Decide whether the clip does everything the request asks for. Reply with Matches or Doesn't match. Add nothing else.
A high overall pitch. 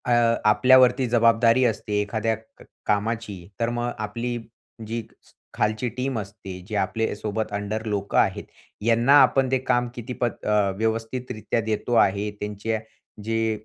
Doesn't match